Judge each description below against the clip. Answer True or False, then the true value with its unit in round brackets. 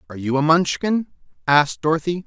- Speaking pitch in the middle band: True (160 Hz)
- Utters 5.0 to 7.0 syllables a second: True (6.3 syllables/s)